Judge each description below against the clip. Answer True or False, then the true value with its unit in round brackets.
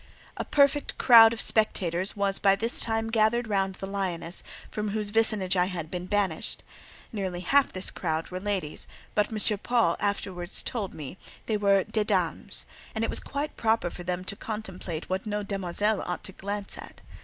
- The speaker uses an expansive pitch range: False (3.1 semitones)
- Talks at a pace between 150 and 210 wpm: True (180 wpm)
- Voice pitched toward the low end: False (200 Hz)